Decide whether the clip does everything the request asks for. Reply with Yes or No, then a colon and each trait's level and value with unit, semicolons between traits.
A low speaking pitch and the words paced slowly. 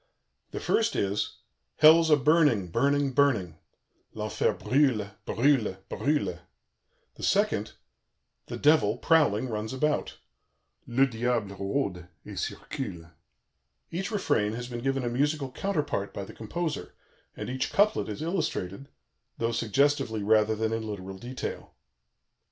Yes: low, 125 Hz; slow, 125 wpm